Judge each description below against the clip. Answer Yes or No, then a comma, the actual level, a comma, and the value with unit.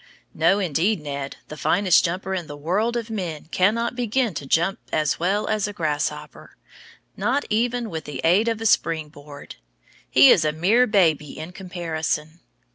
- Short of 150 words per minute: No, average, 170 wpm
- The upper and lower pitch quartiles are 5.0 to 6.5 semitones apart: Yes, wide, 5.6 semitones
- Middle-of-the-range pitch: Yes, medium, 180 Hz